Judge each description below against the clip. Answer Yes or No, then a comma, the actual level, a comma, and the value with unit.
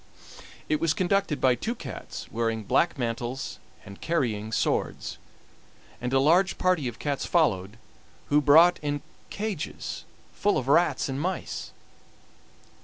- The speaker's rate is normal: No, slow, 130 wpm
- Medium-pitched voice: Yes, medium, 145 Hz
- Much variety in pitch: Yes, wide, 6.2 semitones